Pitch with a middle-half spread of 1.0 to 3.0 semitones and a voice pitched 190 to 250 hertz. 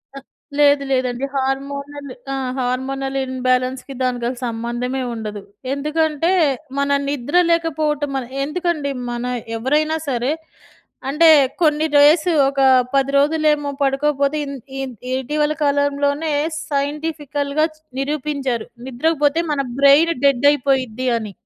No: narrow, 2.4 semitones; very high, 280 Hz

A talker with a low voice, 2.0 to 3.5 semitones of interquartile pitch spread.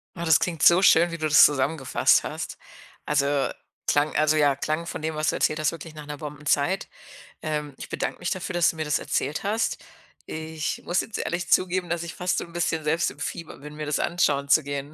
No: medium, 155 Hz; narrow, 2.5 semitones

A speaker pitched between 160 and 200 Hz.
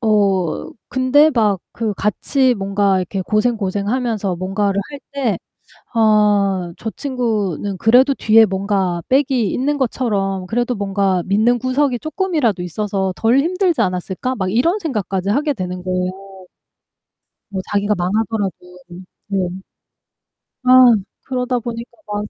No: high, 210 Hz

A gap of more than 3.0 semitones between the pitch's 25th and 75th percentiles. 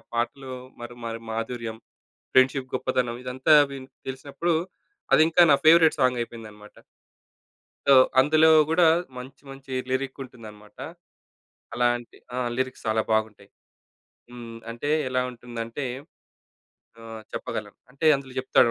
No: average, 2.7 semitones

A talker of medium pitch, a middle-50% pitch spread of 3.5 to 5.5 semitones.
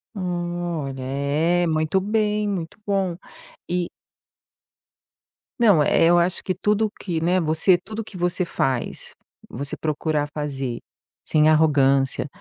Yes: medium, 170 Hz; average, 4.0 semitones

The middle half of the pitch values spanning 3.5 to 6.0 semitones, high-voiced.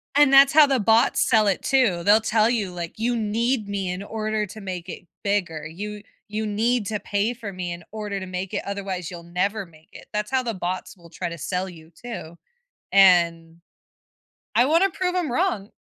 Yes: average, 4.0 semitones; high, 205 Hz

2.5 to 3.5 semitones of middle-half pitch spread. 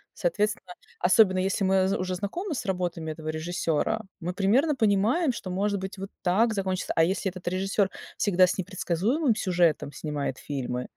Yes: average, 3.0 semitones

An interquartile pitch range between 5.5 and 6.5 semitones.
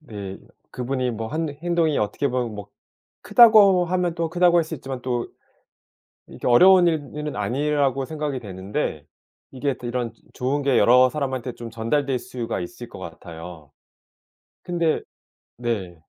No: average, 5.1 semitones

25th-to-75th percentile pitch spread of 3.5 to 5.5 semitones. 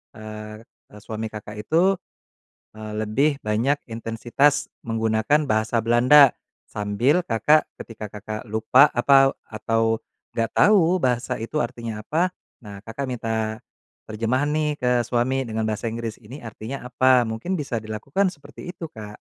Yes: average, 4.2 semitones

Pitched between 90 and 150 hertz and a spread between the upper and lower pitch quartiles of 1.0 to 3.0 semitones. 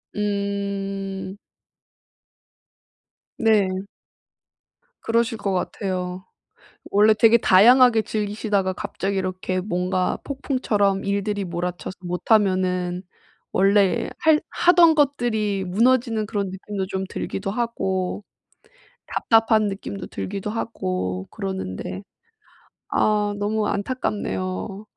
No: high, 200 Hz; narrow, 2.6 semitones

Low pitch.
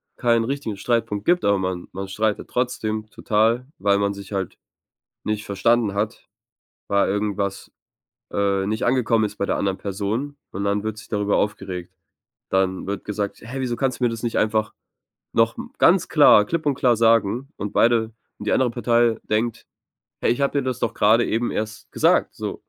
Yes: low, 110 Hz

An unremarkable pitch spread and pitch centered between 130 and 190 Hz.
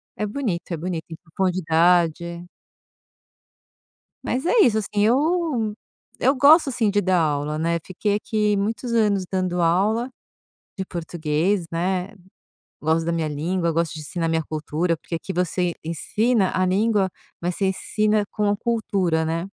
Yes: average, 4.1 semitones; medium, 185 Hz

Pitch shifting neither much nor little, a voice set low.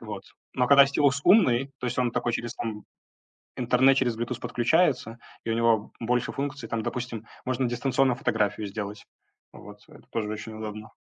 Yes: average, 3.0 semitones; low, 120 Hz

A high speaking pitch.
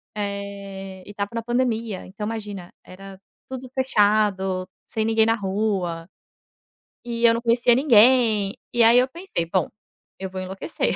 Yes: high, 210 Hz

